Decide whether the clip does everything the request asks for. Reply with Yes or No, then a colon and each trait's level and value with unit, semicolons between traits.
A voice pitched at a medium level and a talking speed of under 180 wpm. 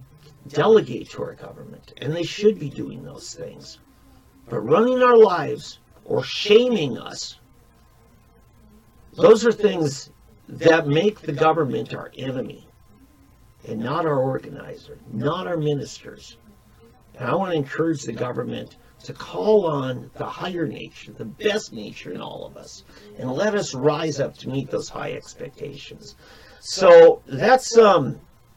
Yes: medium, 150 Hz; average, 140 wpm